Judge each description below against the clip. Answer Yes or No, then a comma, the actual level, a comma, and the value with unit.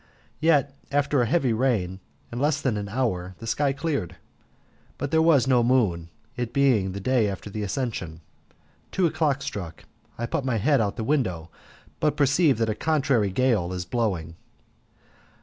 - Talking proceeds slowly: No, average, 170 wpm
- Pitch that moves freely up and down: Yes, wide, 5.9 semitones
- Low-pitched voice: Yes, low, 120 Hz